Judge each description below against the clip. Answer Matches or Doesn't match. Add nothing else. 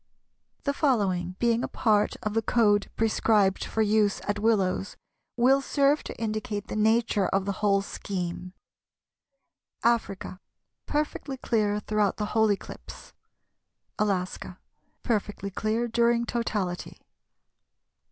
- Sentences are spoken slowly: Matches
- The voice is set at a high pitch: Matches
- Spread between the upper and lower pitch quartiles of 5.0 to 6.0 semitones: Doesn't match